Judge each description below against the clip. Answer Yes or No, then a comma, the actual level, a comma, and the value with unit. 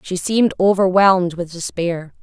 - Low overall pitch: No, medium, 180 Hz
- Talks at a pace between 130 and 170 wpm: Yes, slow, 135 wpm